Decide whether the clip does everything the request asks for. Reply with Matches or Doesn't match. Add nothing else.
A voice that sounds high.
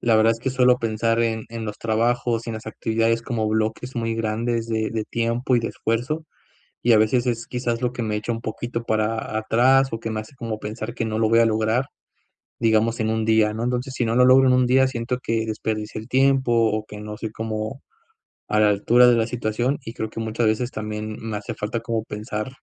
Doesn't match